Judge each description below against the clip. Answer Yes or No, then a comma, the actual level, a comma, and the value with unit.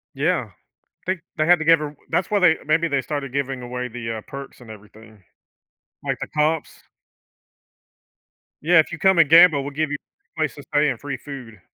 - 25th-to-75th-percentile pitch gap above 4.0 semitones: Yes, average, 4.4 semitones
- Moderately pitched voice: Yes, medium, 145 Hz